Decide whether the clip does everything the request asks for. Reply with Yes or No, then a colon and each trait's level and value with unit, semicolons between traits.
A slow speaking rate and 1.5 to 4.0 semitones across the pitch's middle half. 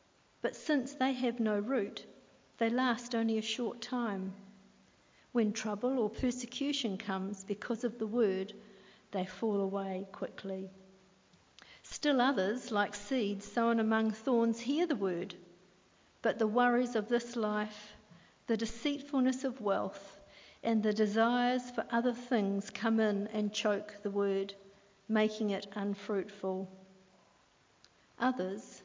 Yes: slow, 125 wpm; average, 3.3 semitones